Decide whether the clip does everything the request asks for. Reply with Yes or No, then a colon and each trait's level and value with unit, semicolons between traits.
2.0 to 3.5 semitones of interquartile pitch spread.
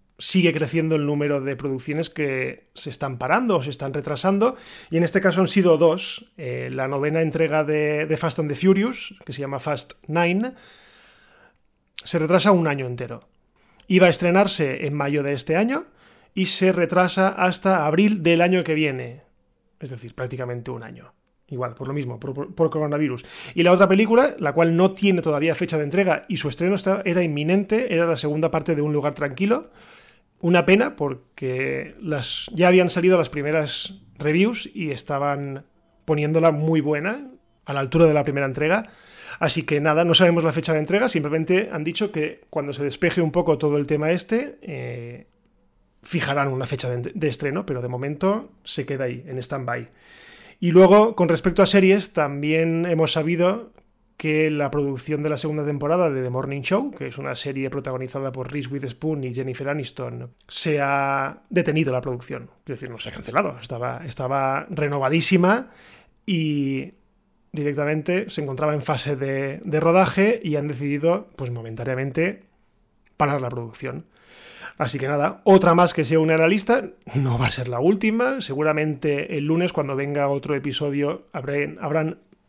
No: average, 4.2 semitones